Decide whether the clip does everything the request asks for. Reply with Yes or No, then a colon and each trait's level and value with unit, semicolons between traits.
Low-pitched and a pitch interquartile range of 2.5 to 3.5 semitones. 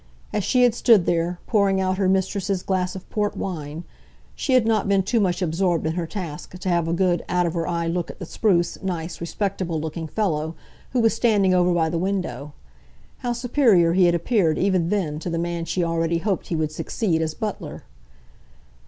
No: medium, 180 Hz; average, 3.0 semitones